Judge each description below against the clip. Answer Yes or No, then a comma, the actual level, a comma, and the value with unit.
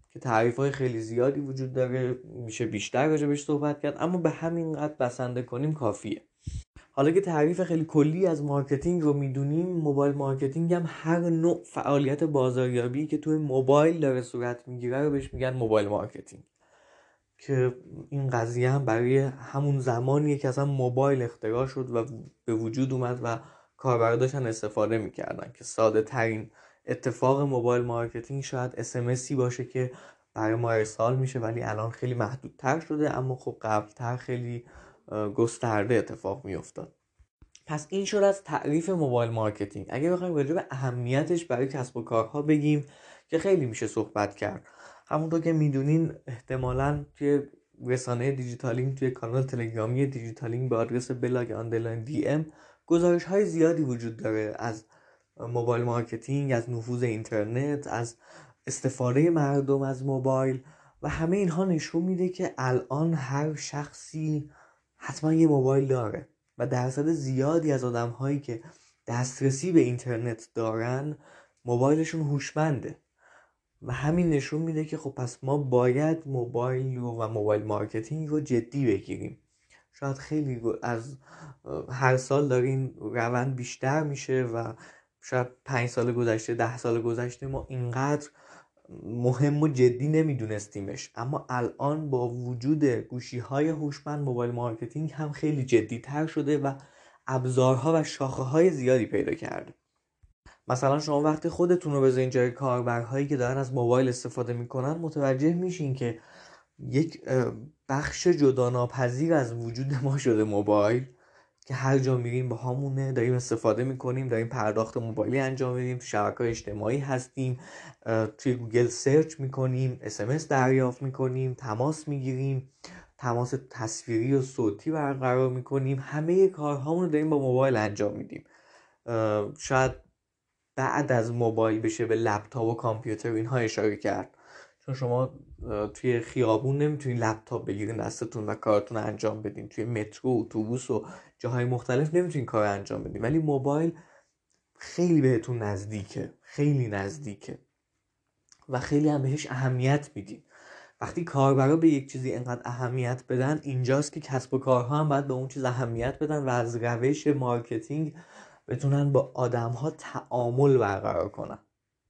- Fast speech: No, average, 140 wpm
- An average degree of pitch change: Yes, average, 3.4 semitones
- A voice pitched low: Yes, low, 130 Hz